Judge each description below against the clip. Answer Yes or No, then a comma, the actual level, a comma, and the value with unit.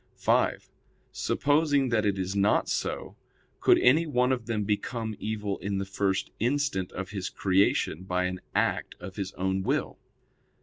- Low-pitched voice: Yes, low, 100 Hz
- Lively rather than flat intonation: No, average, 4.4 semitones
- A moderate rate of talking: Yes, average, 160 wpm